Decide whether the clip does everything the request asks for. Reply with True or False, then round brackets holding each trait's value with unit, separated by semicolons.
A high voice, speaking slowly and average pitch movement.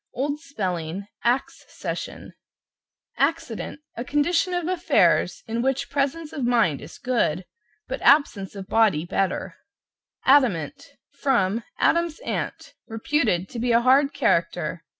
False (255 Hz; 125 wpm; 6.2 semitones)